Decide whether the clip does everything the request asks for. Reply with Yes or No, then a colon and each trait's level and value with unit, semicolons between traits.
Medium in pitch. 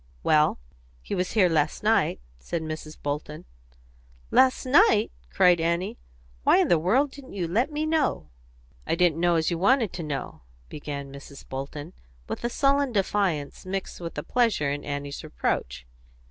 Yes: medium, 170 Hz